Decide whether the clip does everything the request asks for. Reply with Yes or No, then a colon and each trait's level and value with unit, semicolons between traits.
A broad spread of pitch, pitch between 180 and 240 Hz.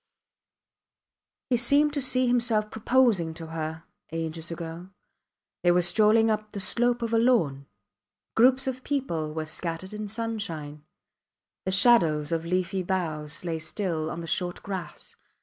Yes: wide, 6.0 semitones; medium, 185 Hz